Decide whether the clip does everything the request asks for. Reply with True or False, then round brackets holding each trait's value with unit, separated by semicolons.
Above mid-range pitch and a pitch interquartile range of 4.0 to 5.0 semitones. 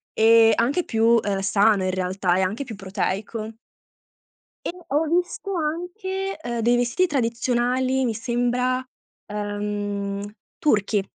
True (230 Hz; 4.3 semitones)